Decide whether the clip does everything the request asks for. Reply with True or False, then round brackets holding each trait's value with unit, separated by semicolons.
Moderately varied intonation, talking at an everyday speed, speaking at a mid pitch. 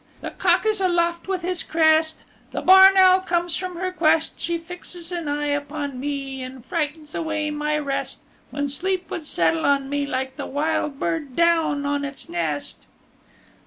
False (3.3 semitones; 170 wpm; 310 Hz)